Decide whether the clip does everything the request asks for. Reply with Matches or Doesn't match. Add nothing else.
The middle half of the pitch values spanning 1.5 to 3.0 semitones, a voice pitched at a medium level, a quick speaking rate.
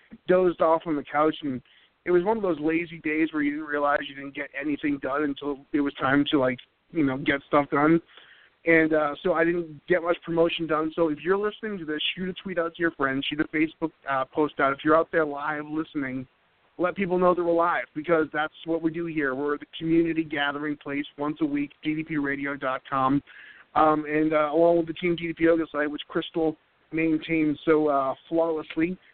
Matches